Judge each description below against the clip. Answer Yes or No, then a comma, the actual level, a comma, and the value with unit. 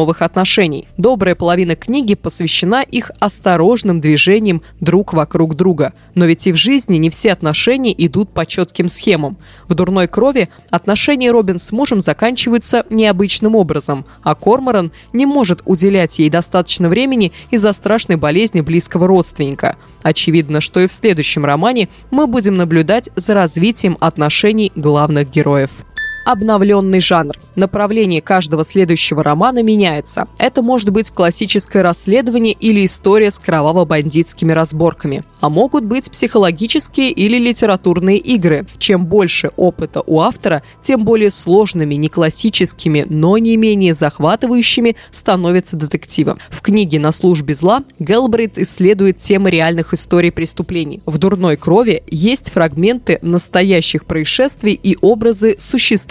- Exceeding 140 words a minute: No, average, 130 wpm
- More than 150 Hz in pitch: Yes, medium, 185 Hz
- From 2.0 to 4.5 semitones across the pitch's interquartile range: No, average, 4.9 semitones